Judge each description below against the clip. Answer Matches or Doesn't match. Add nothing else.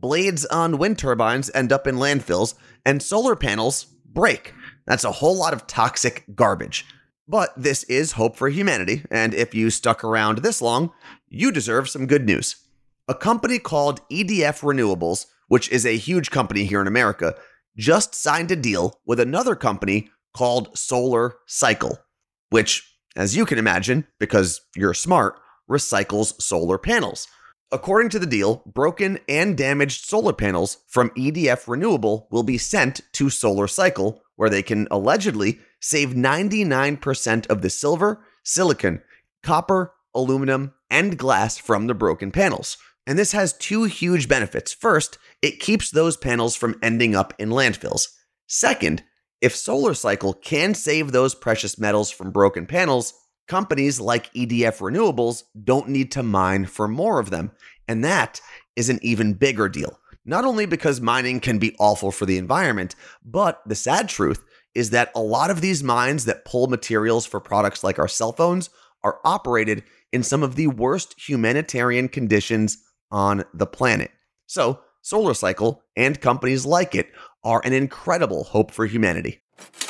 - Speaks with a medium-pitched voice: Doesn't match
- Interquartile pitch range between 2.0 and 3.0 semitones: Doesn't match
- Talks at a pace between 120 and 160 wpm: Matches